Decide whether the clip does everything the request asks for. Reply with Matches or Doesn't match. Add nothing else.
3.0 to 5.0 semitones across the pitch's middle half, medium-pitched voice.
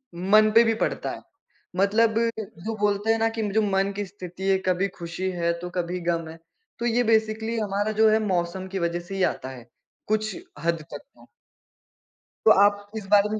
Doesn't match